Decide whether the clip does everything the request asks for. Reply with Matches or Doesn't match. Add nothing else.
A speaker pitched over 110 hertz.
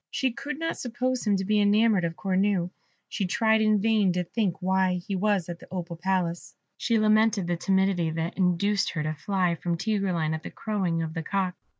Matches